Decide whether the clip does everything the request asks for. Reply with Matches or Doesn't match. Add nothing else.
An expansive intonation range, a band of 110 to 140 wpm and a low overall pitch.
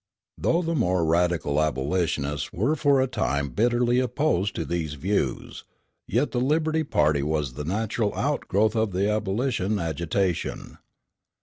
Matches